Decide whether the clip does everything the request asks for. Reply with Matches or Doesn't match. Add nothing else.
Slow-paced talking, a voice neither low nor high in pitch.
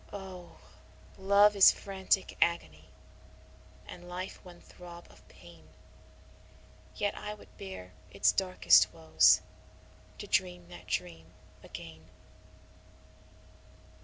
Matches